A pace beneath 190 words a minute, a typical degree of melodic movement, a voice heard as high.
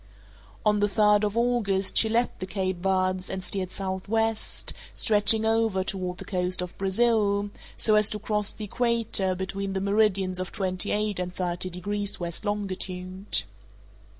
No: average, 155 wpm; narrow, 2.2 semitones; high, 195 Hz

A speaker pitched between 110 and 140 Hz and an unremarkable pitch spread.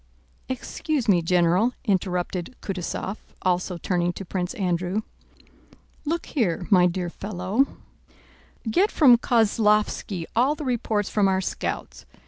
No: high, 195 Hz; average, 4.6 semitones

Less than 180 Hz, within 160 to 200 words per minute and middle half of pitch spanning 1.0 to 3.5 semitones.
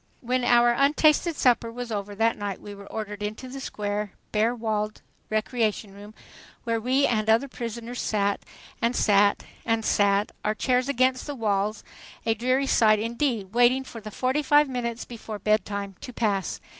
No: high, 225 Hz; average, 170 wpm; average, 3.0 semitones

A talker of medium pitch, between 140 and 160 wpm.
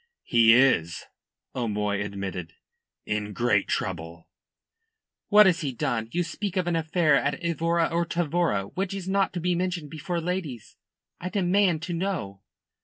Yes: medium, 165 Hz; average, 150 wpm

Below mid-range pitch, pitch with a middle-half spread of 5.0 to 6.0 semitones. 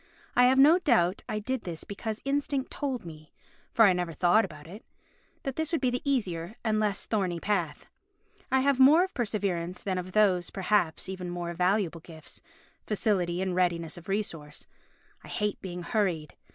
No: high, 195 Hz; wide, 5.4 semitones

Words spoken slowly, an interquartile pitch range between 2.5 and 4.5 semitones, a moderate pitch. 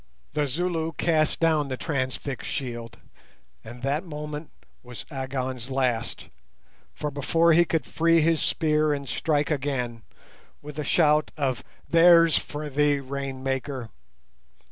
Yes: slow, 130 wpm; average, 3.1 semitones; medium, 145 Hz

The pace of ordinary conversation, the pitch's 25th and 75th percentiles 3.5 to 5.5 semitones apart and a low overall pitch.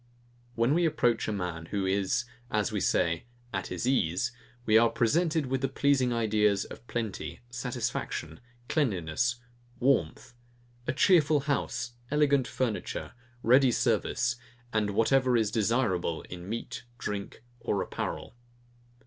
No: slow, 130 wpm; average, 4.6 semitones; low, 115 Hz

